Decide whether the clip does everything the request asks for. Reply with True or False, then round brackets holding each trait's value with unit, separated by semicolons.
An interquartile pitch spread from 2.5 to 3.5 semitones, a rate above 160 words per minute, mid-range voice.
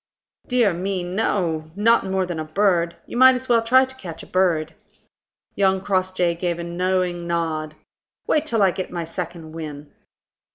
True (3.0 semitones; 170 wpm; 180 Hz)